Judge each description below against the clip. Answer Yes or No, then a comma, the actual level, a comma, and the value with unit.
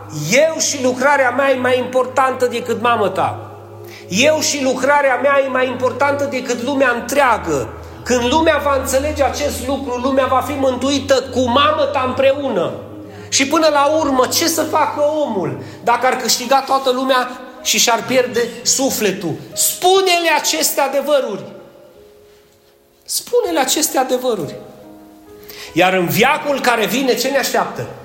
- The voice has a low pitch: No, very high, 255 Hz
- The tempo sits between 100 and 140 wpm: Yes, average, 135 wpm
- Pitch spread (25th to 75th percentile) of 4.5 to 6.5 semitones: Yes, average, 5.0 semitones